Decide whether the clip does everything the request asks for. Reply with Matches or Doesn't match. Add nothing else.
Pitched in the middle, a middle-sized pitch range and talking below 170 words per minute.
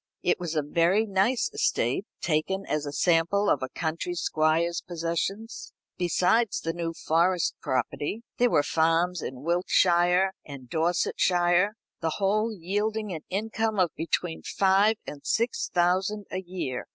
Matches